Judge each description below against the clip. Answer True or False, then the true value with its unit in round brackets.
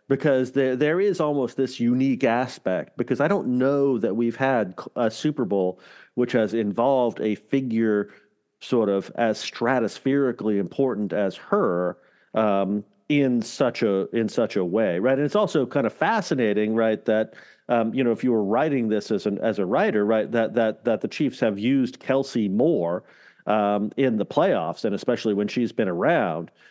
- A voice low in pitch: True (115 Hz)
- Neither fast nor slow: True (180 wpm)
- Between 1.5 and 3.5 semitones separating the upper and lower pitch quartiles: False (4.1 semitones)